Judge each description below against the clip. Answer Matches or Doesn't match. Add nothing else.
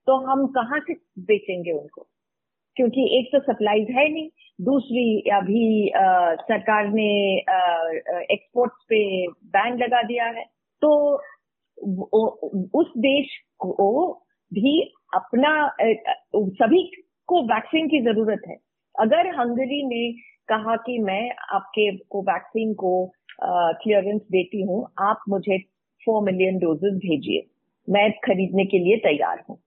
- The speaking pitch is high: Matches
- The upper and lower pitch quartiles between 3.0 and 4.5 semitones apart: Doesn't match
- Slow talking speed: Doesn't match